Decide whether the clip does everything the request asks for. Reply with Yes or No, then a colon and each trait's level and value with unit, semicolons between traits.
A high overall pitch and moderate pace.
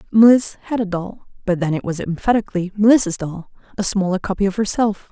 Yes: high, 195 Hz; average, 175 wpm